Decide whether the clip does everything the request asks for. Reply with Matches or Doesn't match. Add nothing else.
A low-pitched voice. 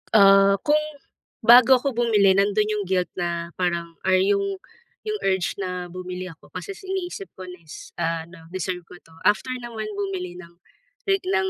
Doesn't match